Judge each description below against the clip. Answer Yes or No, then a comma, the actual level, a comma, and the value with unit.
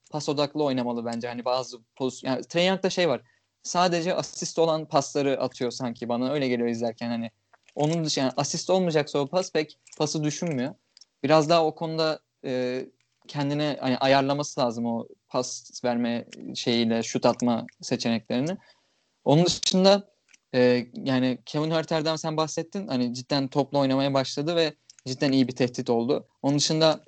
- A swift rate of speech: Yes, fast, 150 wpm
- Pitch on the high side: No, medium, 140 Hz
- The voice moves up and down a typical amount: Yes, average, 4.0 semitones